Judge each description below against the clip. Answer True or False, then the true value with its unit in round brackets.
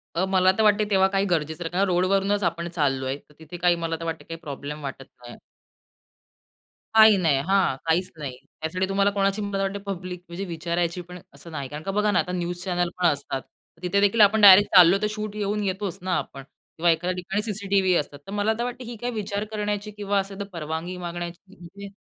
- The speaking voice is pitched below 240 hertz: True (185 Hz)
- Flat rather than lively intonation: False (3.2 semitones)